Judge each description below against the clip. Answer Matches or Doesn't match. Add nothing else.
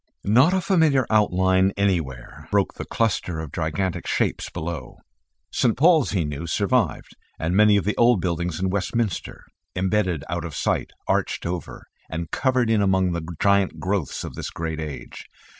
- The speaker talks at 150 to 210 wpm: Matches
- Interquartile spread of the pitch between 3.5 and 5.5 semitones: Matches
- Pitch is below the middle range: Matches